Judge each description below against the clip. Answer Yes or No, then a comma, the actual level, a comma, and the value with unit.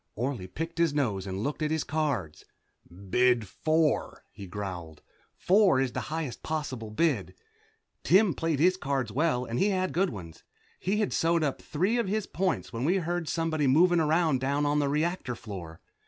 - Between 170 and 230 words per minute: Yes, average, 180 wpm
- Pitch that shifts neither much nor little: No, wide, 6.4 semitones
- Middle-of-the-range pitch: Yes, medium, 145 Hz